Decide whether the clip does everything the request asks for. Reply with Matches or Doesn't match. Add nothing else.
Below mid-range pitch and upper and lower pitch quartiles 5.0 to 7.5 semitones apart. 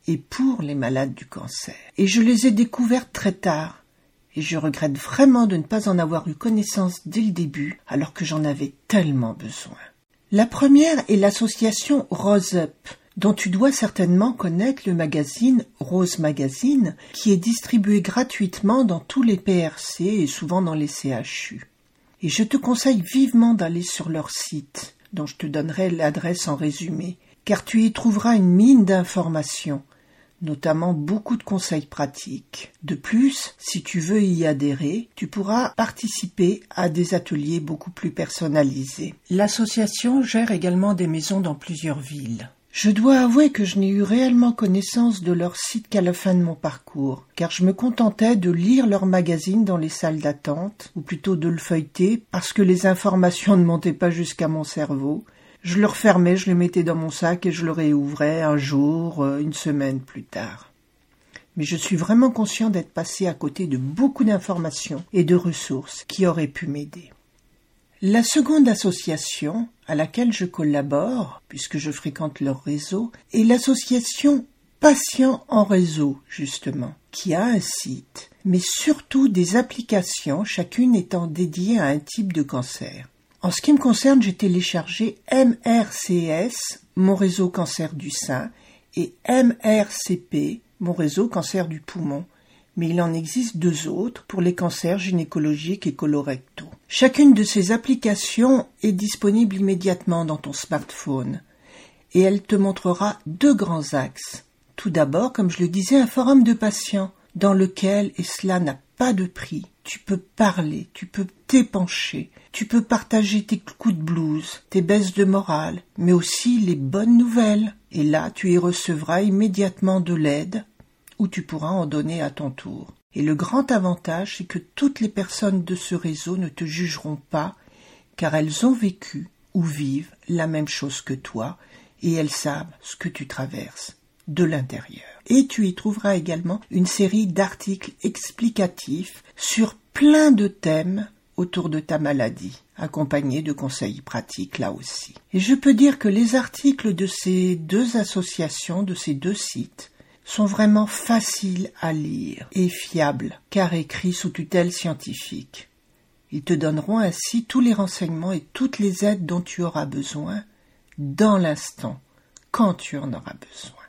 Doesn't match